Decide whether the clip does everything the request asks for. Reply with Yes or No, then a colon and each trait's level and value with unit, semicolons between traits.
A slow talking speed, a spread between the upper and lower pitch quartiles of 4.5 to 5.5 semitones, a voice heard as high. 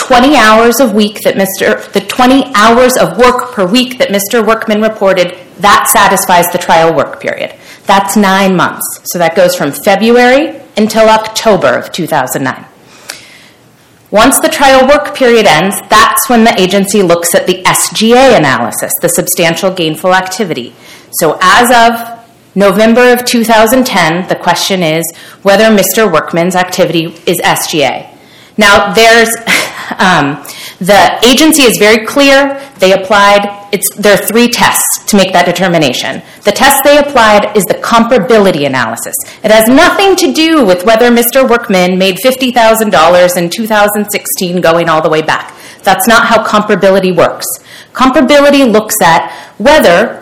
No: average, 155 wpm; average, 4.9 semitones; high, 210 Hz